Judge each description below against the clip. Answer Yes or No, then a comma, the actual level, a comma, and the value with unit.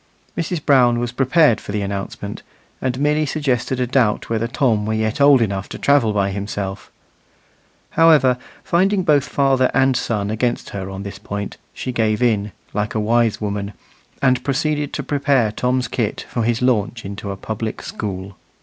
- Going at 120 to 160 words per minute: No, average, 170 wpm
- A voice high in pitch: No, low, 120 Hz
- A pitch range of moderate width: Yes, average, 4.5 semitones